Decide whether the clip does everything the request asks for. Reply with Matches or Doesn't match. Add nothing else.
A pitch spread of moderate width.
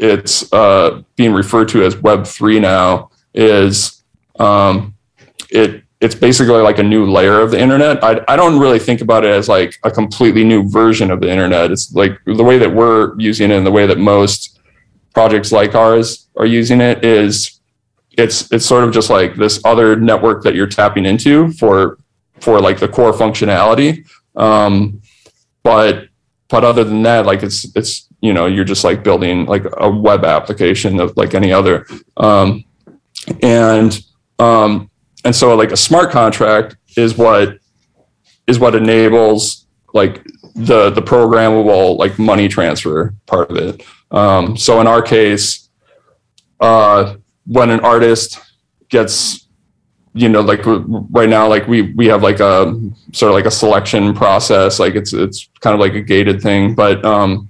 Doesn't match